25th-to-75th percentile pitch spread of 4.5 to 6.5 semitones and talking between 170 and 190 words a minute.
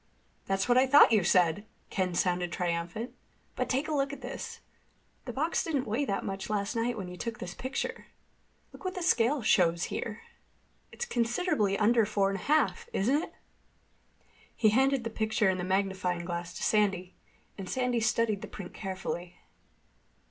Yes: average, 5.3 semitones; average, 175 wpm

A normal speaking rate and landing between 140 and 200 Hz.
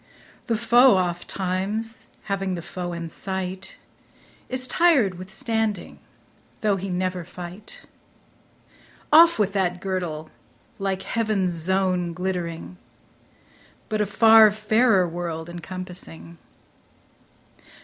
No: slow, 100 wpm; high, 190 Hz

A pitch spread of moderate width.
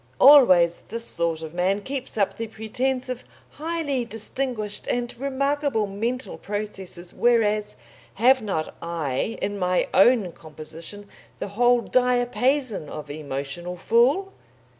No: wide, 5.9 semitones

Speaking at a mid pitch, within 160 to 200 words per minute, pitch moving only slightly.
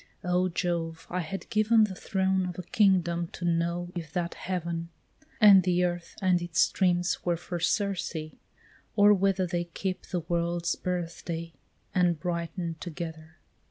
No: medium, 175 Hz; average, 150 wpm; narrow, 1.6 semitones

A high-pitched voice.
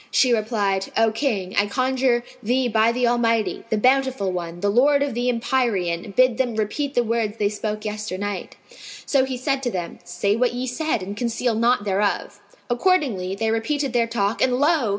Yes: high, 230 Hz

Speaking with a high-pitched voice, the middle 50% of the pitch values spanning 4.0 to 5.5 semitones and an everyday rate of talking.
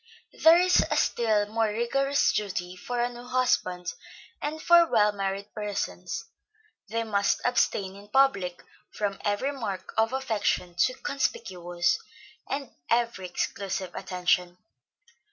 No: high, 215 Hz; average, 4.6 semitones; slow, 125 wpm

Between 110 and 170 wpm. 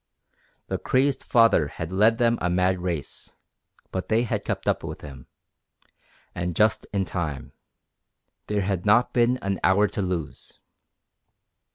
Yes: average, 145 wpm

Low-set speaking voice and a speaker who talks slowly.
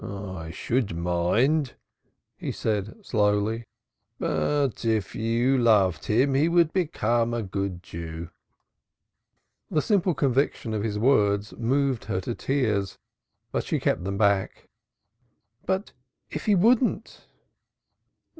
Yes: low, 115 Hz; slow, 115 wpm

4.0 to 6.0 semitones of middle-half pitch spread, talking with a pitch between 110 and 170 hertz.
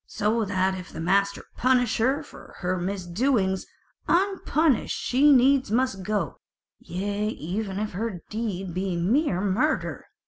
No: average, 5.1 semitones; high, 205 Hz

